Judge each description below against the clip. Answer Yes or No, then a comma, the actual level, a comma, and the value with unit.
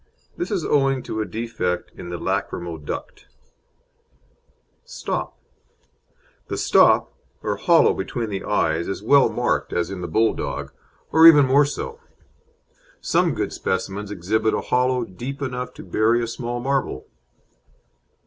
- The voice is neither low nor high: No, low, 115 Hz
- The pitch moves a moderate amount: No, wide, 6.0 semitones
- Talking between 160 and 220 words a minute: No, average, 140 wpm